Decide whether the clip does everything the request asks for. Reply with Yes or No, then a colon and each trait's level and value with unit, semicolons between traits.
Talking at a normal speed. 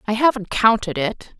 Yes: average, 170 wpm